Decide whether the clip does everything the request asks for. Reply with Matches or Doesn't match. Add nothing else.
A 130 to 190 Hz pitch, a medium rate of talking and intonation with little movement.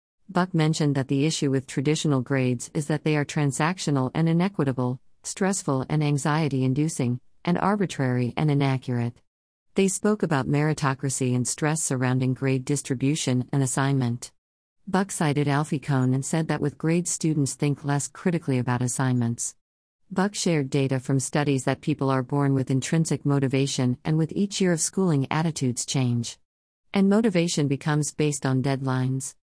Doesn't match